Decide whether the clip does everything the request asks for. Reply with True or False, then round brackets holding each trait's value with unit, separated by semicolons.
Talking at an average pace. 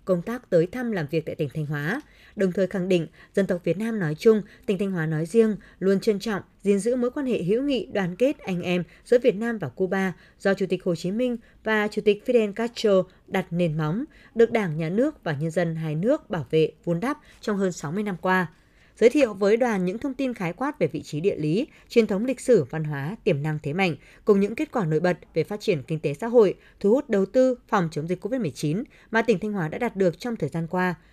False (255 wpm)